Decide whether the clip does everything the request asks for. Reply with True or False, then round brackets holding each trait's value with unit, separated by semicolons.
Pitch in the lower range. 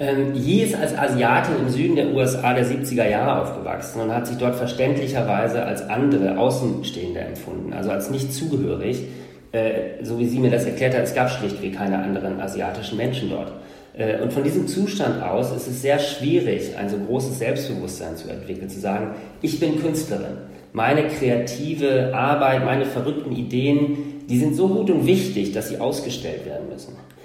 True (125 Hz)